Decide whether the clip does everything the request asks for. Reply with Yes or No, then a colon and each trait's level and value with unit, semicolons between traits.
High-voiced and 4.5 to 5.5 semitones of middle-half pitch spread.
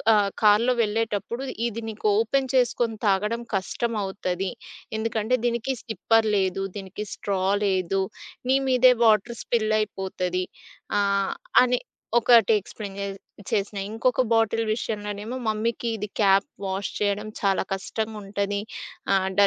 No: high, 210 Hz; average, 2.7 semitones